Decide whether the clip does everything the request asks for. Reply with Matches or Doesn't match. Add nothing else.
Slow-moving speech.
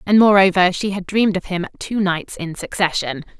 Doesn't match